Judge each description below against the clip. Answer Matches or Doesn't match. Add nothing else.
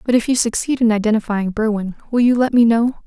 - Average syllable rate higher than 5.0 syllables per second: Matches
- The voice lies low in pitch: Doesn't match